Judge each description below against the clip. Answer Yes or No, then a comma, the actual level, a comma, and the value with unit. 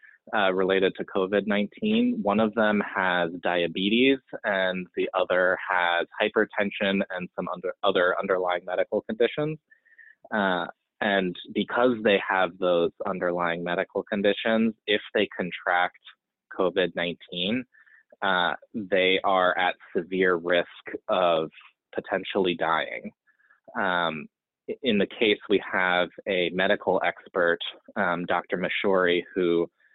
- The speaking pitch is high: No, very low, 95 Hz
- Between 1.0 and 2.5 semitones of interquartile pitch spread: No, average, 2.9 semitones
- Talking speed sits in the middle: No, slow, 115 wpm